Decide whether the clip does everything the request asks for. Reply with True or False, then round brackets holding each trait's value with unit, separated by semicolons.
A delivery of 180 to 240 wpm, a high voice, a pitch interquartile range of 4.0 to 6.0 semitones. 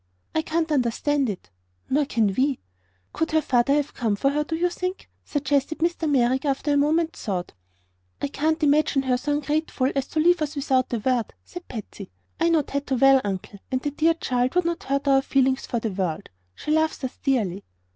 False (200 wpm; 280 Hz; 3.6 semitones)